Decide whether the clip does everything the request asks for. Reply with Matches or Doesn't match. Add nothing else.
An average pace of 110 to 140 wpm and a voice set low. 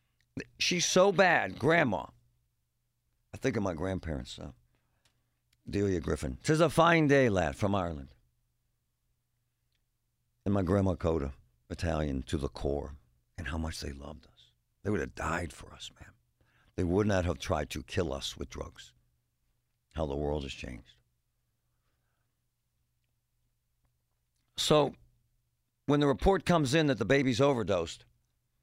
Matches